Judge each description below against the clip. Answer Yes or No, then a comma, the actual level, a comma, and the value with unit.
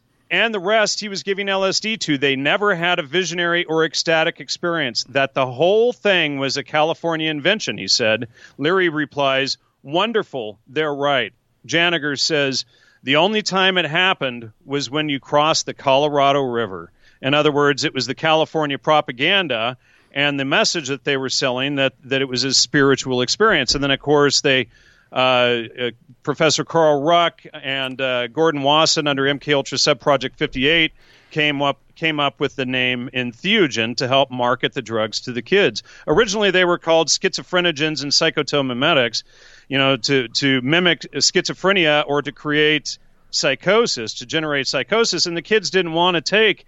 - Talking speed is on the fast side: No, average, 165 wpm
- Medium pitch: Yes, medium, 145 Hz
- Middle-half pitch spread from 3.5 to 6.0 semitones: Yes, average, 3.8 semitones